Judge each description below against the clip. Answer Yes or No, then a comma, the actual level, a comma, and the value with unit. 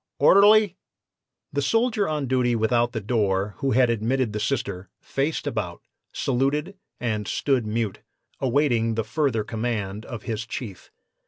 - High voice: No, low, 120 Hz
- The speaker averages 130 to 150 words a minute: Yes, average, 140 wpm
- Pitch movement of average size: Yes, average, 4.2 semitones